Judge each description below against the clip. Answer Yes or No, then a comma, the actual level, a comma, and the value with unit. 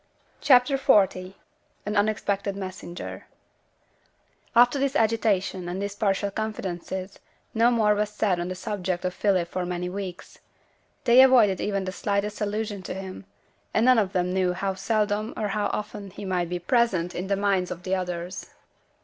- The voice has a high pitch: Yes, high, 200 Hz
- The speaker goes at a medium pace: Yes, average, 165 wpm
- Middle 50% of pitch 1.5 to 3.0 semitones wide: Yes, narrow, 2.6 semitones